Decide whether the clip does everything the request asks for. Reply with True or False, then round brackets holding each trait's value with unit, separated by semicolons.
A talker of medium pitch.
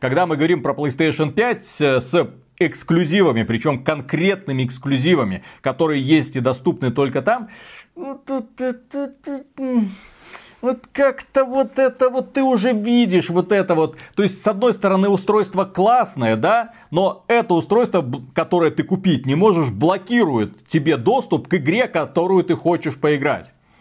True (180 Hz)